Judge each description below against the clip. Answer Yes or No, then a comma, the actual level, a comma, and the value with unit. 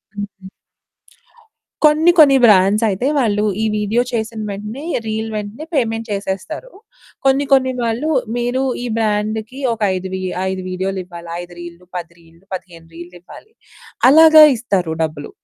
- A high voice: Yes, high, 210 Hz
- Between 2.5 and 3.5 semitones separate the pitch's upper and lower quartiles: No, average, 5.1 semitones